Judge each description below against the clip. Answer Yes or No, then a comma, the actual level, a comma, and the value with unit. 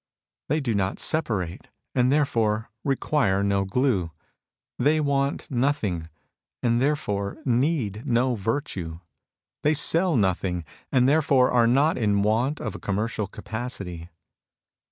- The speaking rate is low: Yes, slow, 120 wpm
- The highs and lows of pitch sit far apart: Yes, wide, 5.8 semitones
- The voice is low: Yes, low, 120 Hz